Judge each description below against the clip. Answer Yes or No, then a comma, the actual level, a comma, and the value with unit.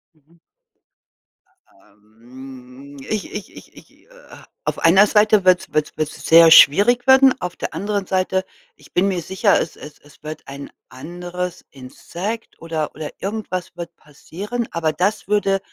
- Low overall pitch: No, medium, 175 Hz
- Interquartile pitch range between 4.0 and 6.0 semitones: Yes, average, 5.0 semitones